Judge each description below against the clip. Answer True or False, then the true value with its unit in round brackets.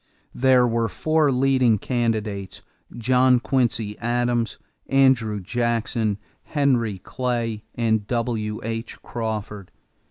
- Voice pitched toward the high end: False (115 Hz)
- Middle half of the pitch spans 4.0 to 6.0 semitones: False (2.5 semitones)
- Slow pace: True (90 wpm)